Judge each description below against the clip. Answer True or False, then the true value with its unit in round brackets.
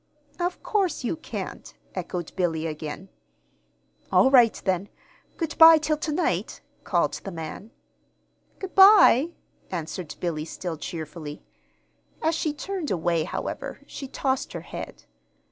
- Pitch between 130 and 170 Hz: False (205 Hz)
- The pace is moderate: False (130 wpm)